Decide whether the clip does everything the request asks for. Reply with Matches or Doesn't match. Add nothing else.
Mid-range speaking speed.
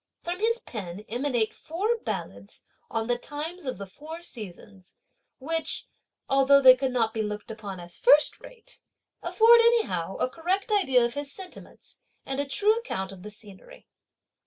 Matches